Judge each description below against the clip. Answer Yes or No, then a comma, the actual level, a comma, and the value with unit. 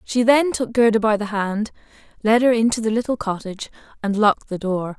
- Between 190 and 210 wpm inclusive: Yes, fast, 205 wpm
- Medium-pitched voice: No, high, 220 Hz